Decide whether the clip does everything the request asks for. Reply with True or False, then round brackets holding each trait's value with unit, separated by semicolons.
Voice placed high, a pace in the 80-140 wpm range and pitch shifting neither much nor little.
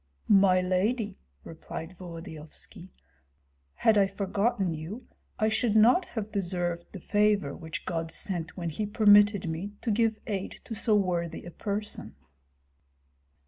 True (195 Hz; 135 wpm; 3.7 semitones)